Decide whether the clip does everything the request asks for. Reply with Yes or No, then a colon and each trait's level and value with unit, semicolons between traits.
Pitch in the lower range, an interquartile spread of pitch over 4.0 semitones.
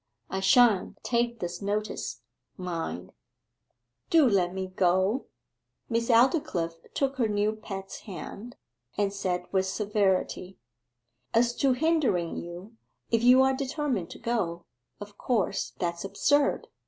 No: high, 205 Hz; average, 4.5 semitones